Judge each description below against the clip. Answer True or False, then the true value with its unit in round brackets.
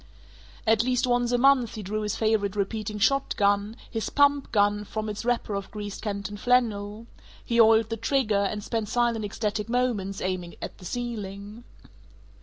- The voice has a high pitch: True (215 Hz)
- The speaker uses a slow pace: False (165 wpm)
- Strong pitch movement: False (2.7 semitones)